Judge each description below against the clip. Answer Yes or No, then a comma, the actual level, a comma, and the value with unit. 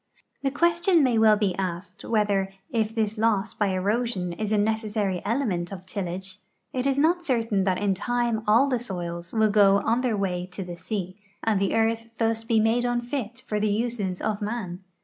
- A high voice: Yes, high, 215 Hz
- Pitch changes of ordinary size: Yes, average, 3.4 semitones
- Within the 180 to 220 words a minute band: Yes, average, 190 wpm